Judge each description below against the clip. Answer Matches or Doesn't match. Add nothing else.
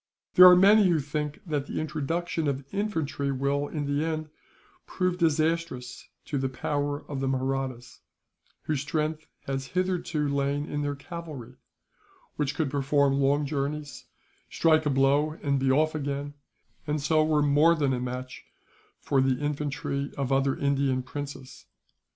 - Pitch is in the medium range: Matches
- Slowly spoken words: Doesn't match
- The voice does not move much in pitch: Matches